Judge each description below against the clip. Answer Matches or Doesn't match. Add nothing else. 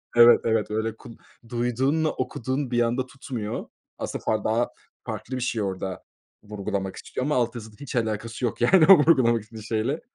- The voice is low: Matches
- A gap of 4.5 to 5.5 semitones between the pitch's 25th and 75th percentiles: Doesn't match